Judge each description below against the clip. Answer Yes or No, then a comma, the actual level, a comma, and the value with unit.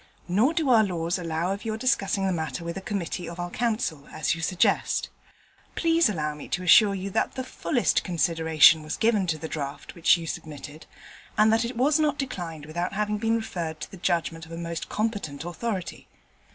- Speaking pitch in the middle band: Yes, medium, 180 Hz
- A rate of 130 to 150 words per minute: No, average, 200 wpm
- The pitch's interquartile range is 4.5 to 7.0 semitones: Yes, average, 5.1 semitones